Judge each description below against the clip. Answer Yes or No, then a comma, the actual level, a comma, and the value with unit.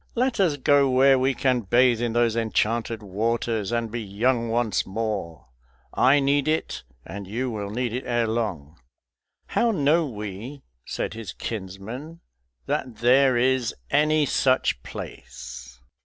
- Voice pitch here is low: Yes, low, 120 Hz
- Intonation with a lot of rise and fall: No, average, 4.0 semitones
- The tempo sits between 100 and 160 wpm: Yes, average, 140 wpm